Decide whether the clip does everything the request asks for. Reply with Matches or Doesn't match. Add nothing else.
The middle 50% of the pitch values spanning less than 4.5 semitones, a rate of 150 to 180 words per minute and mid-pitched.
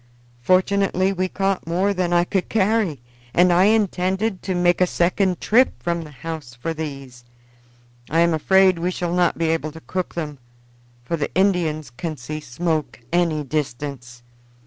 Matches